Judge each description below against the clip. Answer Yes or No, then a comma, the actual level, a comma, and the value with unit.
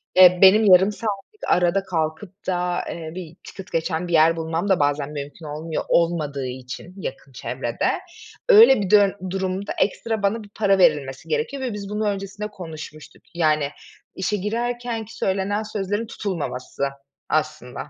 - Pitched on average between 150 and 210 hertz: Yes, medium, 185 Hz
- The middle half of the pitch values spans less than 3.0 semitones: No, average, 4.5 semitones